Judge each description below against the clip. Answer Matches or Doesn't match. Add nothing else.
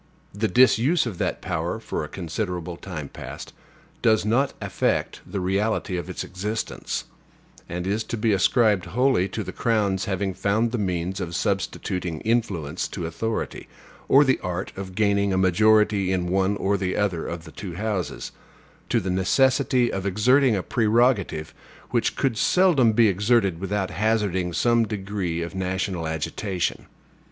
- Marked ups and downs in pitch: Doesn't match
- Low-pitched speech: Matches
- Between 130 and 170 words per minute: Matches